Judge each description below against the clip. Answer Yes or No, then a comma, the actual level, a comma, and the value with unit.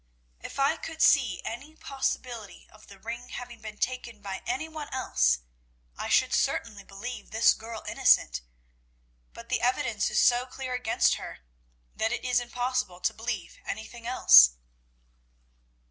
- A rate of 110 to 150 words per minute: Yes, average, 145 wpm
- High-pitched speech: Yes, high, 235 Hz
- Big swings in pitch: No, average, 3.2 semitones